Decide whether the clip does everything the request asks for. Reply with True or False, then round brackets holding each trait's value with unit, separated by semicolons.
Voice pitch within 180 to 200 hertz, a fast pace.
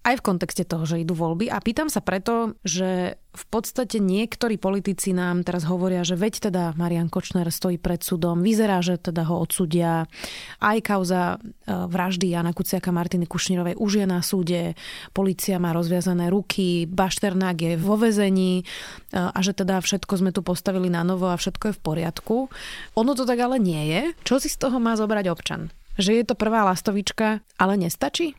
True (185 Hz; 180 wpm)